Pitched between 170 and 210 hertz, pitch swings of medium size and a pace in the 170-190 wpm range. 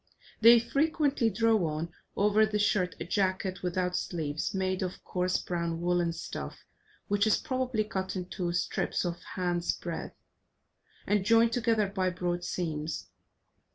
No: medium, 185 Hz; average, 3.7 semitones; average, 145 wpm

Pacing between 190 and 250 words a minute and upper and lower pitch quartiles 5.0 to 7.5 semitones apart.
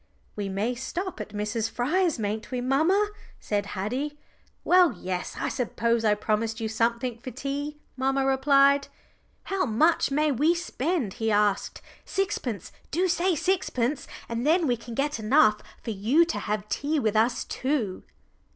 No: average, 155 wpm; wide, 5.6 semitones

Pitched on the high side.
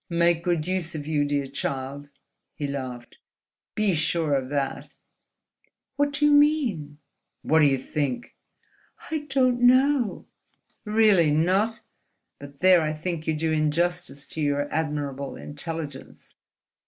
No: medium, 160 Hz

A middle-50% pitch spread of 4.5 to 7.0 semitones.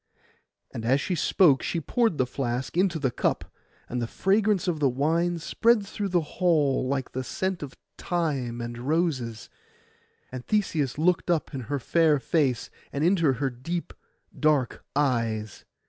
Yes: average, 5.2 semitones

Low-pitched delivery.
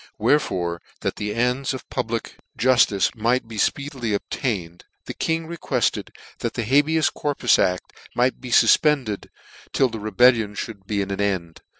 Yes: low, 115 Hz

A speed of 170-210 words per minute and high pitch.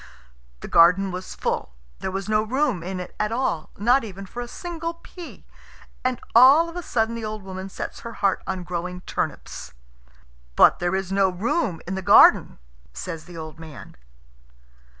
Yes: average, 175 wpm; high, 195 Hz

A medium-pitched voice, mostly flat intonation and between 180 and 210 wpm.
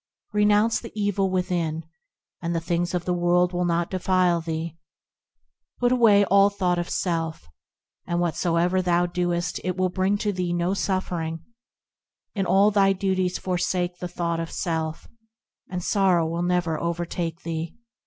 No: medium, 180 Hz; narrow, 1.9 semitones; average, 155 wpm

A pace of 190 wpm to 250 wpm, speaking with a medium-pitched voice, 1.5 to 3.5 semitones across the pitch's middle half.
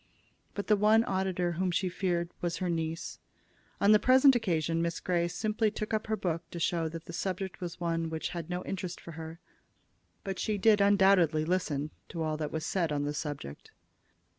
Yes: average, 195 wpm; medium, 175 Hz; average, 3.2 semitones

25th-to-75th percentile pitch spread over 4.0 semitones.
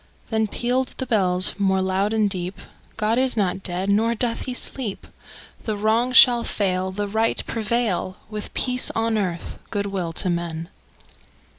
No: average, 3.4 semitones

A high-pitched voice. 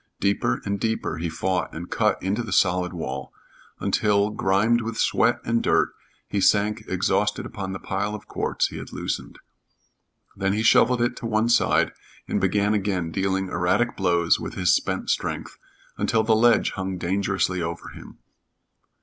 No: low, 100 Hz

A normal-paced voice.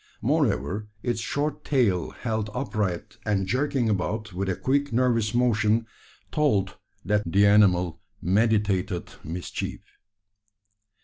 No: slow, 110 wpm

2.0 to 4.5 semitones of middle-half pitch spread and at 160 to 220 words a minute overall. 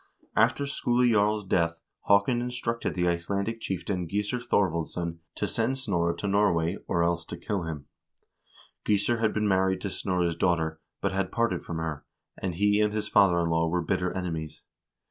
Yes: average, 3.8 semitones; average, 180 wpm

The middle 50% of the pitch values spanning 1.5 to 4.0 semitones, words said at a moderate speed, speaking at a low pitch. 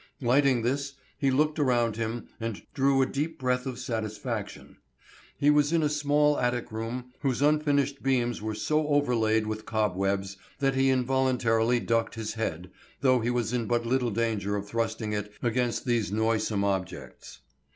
Yes: average, 3.5 semitones; average, 160 wpm; low, 120 Hz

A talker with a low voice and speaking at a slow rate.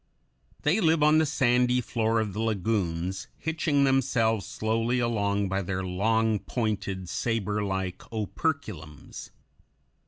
Yes: low, 110 Hz; slow, 115 wpm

